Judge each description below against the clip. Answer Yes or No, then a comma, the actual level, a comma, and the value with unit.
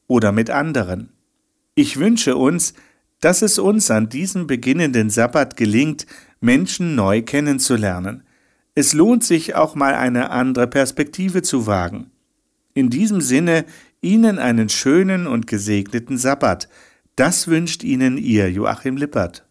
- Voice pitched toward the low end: No, medium, 145 Hz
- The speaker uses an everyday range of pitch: No, wide, 8.1 semitones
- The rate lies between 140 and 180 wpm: No, average, 130 wpm